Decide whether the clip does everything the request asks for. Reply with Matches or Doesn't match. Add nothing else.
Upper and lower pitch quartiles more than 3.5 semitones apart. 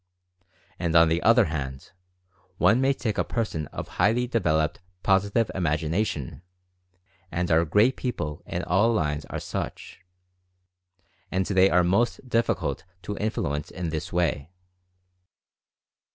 Matches